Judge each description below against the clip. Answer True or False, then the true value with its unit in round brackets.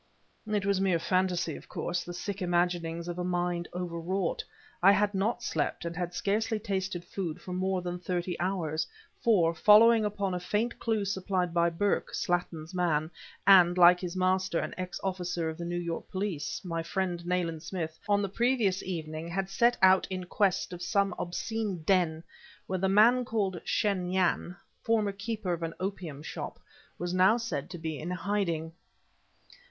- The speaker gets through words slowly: False (170 wpm)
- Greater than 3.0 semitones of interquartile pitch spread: False (2.5 semitones)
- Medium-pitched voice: True (180 Hz)